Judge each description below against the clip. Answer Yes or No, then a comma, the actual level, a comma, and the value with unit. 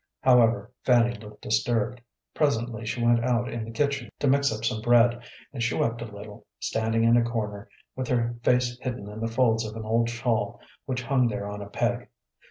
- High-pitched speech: No, low, 115 Hz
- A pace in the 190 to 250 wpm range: Yes, average, 200 wpm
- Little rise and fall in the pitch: Yes, narrow, 1.7 semitones